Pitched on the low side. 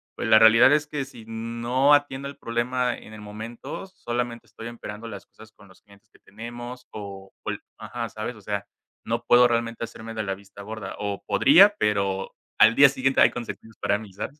Yes: low, 115 Hz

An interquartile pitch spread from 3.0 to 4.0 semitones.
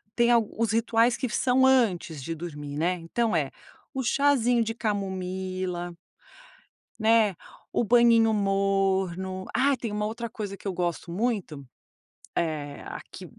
No: average, 4.6 semitones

